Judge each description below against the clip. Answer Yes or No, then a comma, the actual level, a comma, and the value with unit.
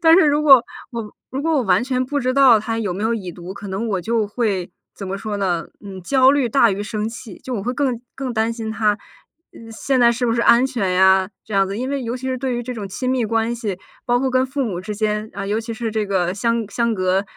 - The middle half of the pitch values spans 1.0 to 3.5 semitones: No, average, 4.0 semitones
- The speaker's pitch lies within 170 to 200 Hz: No, high, 225 Hz